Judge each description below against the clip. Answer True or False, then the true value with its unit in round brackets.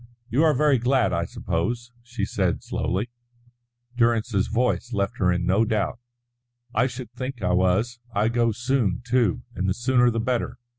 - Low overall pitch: True (120 Hz)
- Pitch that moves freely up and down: False (3.6 semitones)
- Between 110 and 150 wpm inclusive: False (165 wpm)